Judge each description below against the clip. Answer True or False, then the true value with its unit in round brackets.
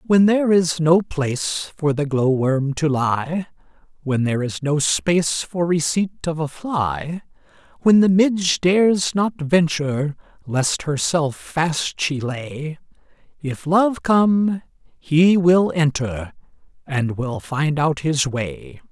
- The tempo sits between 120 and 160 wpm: True (140 wpm)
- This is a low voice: False (160 Hz)